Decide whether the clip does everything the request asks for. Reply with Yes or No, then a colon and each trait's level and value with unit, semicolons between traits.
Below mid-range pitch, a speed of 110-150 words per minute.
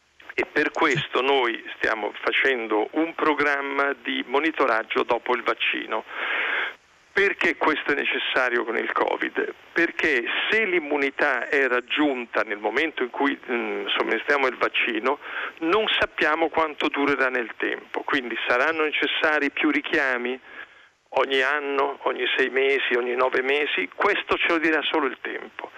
No: medium, 150 Hz; average, 135 wpm